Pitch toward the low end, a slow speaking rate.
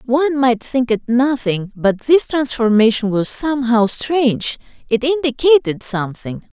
No: very high, 250 Hz; slow, 130 wpm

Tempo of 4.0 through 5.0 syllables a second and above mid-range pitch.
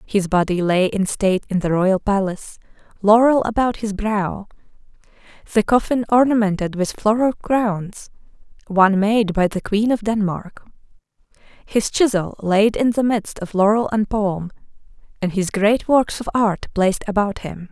Yes: 4.6 syllables/s; high, 205 Hz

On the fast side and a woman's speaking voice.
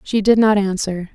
Yes: fast, 210 wpm; female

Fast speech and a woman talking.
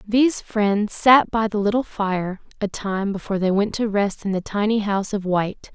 Yes: fast, 210 wpm; female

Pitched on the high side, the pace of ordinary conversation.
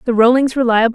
Yes: high, 240 Hz; average, 190 wpm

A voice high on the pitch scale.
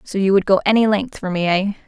Yes: high, 200 Hz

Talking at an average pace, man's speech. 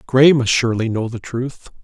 Yes: average, 195 wpm; male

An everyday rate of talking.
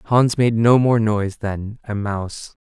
Yes: average, 185 wpm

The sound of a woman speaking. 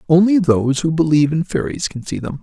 No: male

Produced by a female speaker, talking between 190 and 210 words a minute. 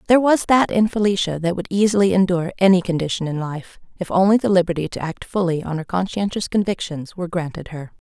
Yes: female; average, 200 wpm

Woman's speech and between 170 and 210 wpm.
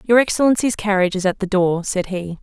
No: female; fast, 225 wpm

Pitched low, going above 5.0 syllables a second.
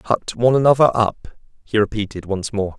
Yes: low, 110 Hz; 5.3 syllables/s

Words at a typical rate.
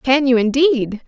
Yes: average, 165 wpm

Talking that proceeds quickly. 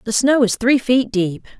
Yes: fast, 225 wpm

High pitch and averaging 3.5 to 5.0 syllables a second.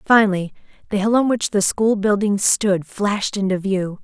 Yes: high, 200 Hz; 4.8 syllables/s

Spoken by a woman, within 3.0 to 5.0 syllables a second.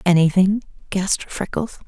Yes: female; 4.8 syllables/s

